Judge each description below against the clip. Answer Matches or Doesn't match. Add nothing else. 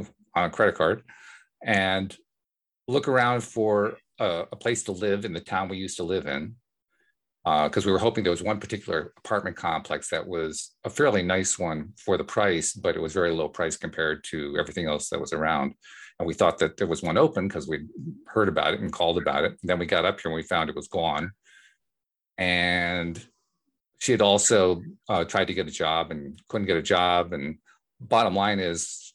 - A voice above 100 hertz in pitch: Doesn't match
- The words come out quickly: Matches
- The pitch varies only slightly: Doesn't match